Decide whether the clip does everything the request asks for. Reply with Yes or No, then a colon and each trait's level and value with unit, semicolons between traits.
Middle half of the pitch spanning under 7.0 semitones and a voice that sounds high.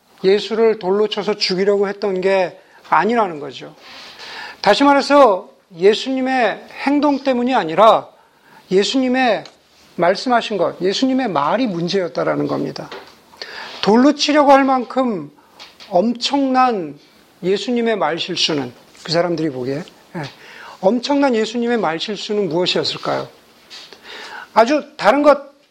Yes: wide, 6.4 semitones; high, 230 Hz